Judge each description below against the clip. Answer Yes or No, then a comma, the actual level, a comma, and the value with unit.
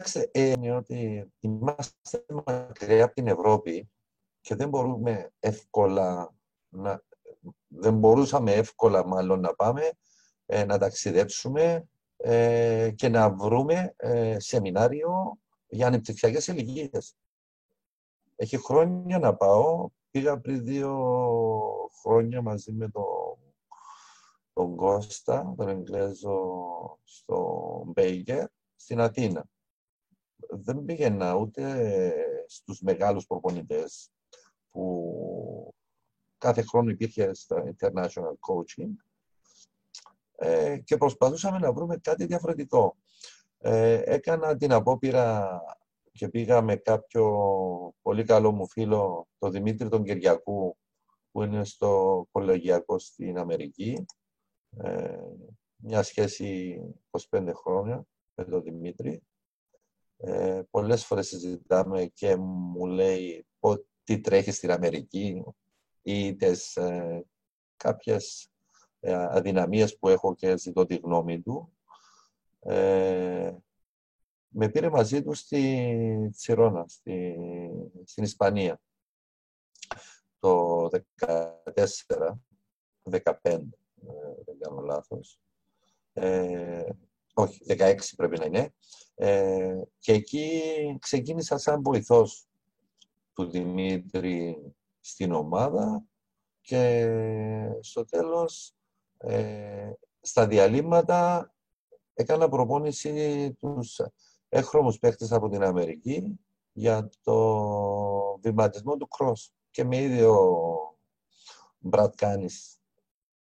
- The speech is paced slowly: Yes, slow, 95 wpm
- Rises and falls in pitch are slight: No, wide, 7.4 semitones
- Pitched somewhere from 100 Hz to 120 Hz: Yes, low, 115 Hz